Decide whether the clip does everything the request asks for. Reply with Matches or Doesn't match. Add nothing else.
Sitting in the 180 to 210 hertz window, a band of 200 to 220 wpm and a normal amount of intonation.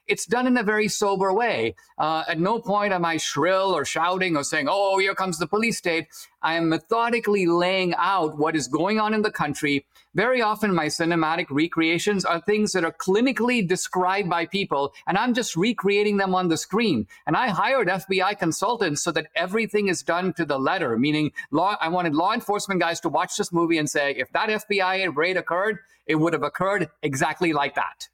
Matches